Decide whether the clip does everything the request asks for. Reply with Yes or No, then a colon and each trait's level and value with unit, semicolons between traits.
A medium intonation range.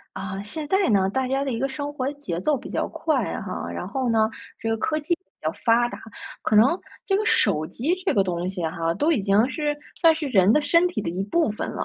No: wide, 7.6 semitones